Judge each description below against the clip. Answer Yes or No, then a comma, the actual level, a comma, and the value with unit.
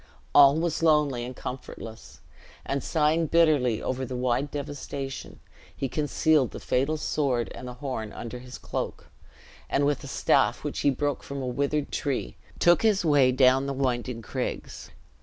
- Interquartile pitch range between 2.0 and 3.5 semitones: Yes, average, 2.9 semitones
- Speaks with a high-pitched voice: No, medium, 140 Hz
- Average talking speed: Yes, average, 160 wpm